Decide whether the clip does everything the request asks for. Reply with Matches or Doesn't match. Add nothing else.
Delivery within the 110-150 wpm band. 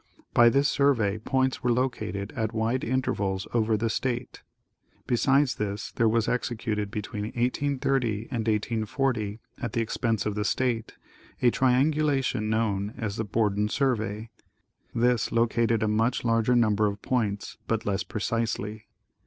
Matches